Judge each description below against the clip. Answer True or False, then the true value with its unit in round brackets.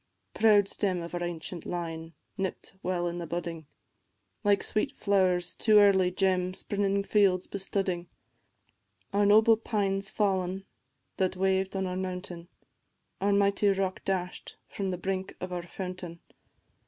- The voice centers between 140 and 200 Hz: True (190 Hz)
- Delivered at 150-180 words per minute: False (140 wpm)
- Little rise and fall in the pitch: True (2.0 semitones)